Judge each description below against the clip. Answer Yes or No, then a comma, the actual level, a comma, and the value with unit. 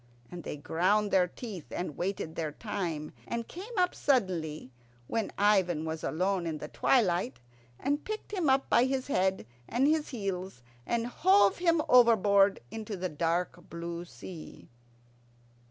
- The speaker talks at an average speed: Yes, average, 150 wpm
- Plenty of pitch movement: Yes, wide, 6.1 semitones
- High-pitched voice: Yes, high, 195 Hz